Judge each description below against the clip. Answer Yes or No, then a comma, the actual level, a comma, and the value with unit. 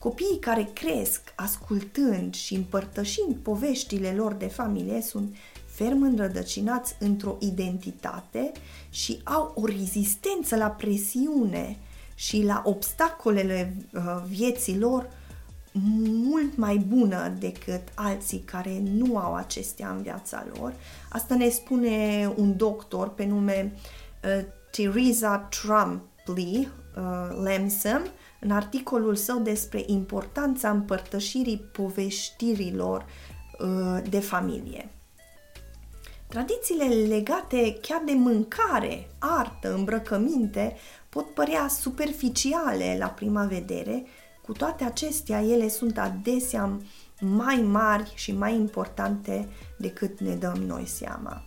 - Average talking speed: No, slow, 105 wpm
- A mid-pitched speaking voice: No, high, 210 Hz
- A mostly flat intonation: No, average, 3.8 semitones